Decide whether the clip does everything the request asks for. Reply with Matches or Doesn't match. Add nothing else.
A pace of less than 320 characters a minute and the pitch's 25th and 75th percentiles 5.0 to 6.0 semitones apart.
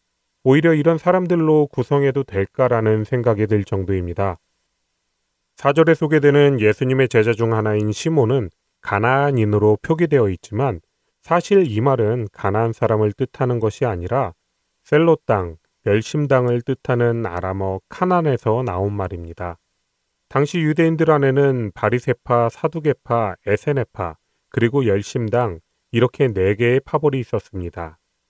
Matches